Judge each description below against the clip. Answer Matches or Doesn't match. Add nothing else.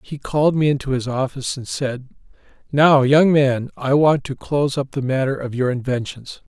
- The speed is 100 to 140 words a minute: Doesn't match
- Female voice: Doesn't match